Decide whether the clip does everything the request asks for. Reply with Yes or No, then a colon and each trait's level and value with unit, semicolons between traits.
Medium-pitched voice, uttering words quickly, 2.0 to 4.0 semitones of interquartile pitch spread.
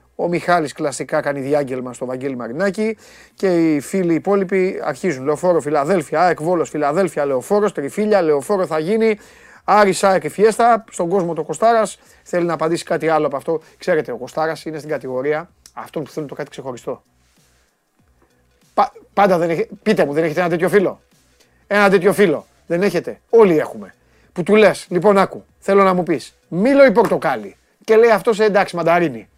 No: medium, 175 Hz; fast, 175 wpm; average, 5.1 semitones